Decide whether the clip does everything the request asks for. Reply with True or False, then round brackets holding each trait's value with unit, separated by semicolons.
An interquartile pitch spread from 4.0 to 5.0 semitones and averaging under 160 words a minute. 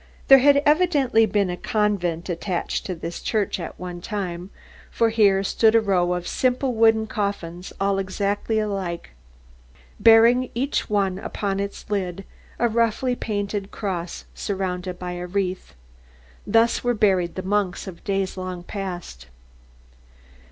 False (3.6 semitones; 140 wpm)